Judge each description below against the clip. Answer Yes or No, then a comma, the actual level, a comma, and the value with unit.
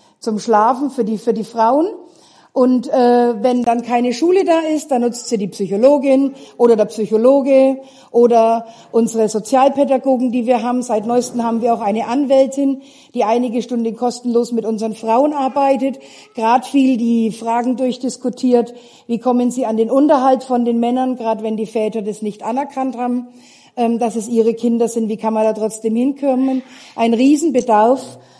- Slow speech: No, average, 170 wpm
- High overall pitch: Yes, high, 245 Hz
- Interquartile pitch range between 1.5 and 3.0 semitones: Yes, narrow, 2.6 semitones